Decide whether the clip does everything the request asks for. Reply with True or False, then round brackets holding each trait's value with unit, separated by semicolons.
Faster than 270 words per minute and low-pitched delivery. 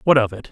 True (350 wpm; 120 Hz)